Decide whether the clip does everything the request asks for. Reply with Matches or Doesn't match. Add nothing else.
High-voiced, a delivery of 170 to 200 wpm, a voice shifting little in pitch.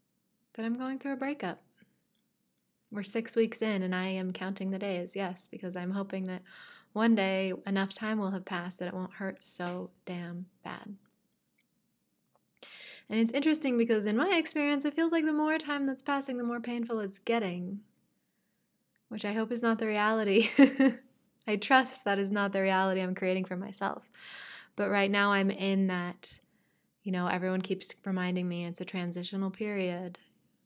Doesn't match